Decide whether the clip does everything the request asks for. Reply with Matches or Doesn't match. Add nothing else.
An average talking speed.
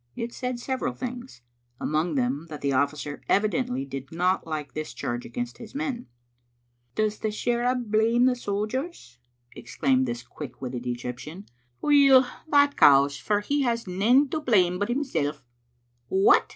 Matches